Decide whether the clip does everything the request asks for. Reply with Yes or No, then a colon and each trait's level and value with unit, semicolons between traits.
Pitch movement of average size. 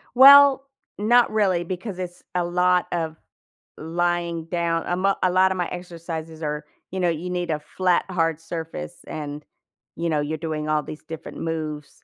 No: narrow, 2.2 semitones